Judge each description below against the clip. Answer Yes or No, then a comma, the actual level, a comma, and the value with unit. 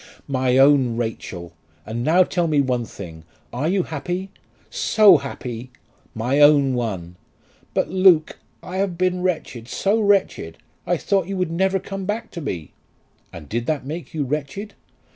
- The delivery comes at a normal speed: Yes, average, 160 wpm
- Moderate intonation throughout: No, wide, 7.3 semitones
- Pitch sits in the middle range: Yes, medium, 150 Hz